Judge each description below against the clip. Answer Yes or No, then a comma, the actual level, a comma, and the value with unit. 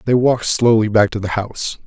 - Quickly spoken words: Yes, fast, 225 wpm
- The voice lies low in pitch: Yes, low, 110 Hz